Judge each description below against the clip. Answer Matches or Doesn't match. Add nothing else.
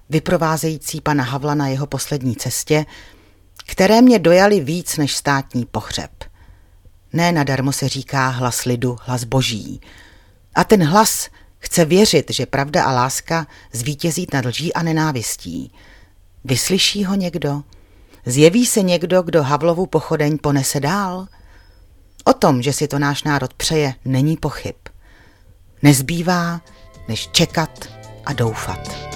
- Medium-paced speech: Matches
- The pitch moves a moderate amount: Doesn't match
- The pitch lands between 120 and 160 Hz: Matches